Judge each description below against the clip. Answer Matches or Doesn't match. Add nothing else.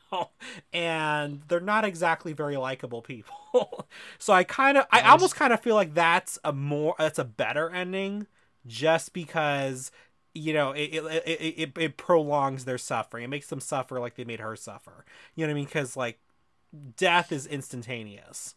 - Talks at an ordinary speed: Matches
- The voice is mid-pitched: Matches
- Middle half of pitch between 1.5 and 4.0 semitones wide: Doesn't match